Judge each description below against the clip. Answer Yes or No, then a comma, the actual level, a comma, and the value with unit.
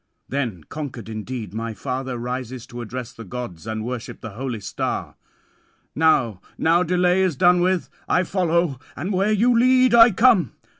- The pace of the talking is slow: No, average, 160 wpm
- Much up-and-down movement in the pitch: Yes, wide, 7.5 semitones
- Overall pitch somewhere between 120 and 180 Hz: Yes, low, 135 Hz